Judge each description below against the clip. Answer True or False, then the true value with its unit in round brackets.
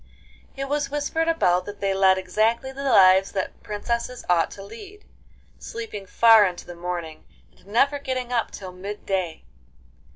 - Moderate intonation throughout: False (5.9 semitones)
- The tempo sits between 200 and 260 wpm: False (160 wpm)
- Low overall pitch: False (210 Hz)